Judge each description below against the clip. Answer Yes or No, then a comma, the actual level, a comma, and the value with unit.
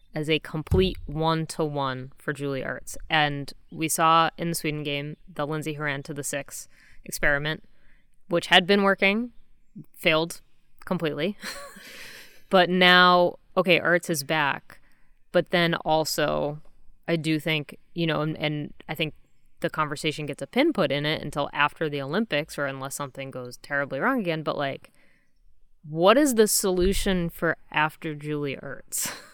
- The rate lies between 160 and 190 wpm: No, average, 150 wpm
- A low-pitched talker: No, medium, 155 Hz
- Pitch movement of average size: Yes, average, 3.3 semitones